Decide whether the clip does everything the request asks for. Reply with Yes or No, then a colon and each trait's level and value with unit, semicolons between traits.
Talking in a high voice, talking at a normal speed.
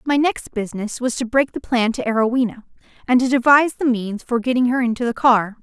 No: high, 245 Hz; fast, 225 wpm